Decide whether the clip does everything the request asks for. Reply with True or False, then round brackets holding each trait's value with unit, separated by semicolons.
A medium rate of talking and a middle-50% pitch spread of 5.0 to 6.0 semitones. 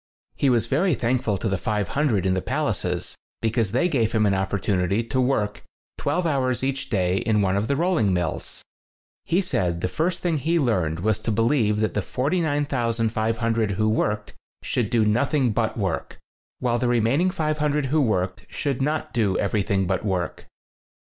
True (170 wpm; 5.3 semitones)